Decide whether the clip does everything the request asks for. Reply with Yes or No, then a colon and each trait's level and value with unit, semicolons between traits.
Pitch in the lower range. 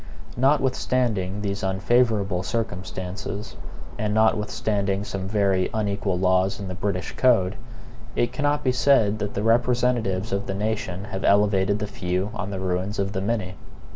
Yes: low, 100 Hz